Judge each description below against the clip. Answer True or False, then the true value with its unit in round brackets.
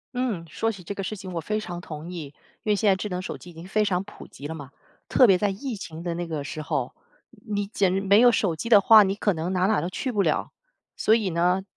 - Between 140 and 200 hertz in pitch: True (190 Hz)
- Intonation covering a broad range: False (3.6 semitones)